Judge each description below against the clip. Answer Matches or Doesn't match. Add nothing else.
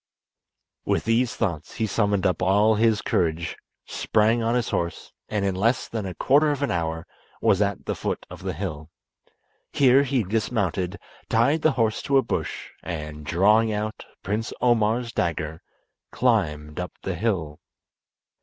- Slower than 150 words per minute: Doesn't match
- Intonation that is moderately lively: Matches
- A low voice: Matches